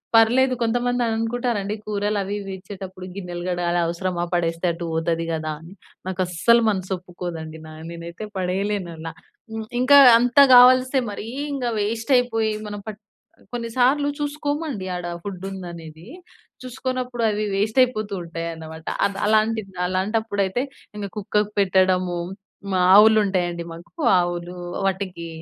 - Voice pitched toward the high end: Yes, high, 200 Hz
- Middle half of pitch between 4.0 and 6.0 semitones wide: Yes, average, 4.4 semitones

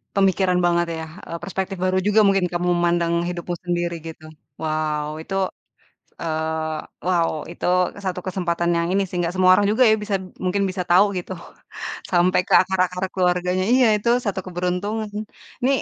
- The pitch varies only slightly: Yes, narrow, 1.8 semitones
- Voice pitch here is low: No, medium, 180 Hz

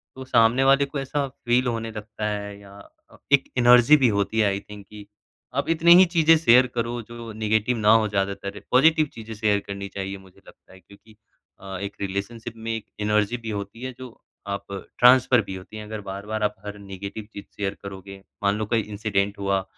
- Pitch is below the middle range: Yes, low, 110 Hz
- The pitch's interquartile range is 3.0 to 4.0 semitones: Yes, average, 3.3 semitones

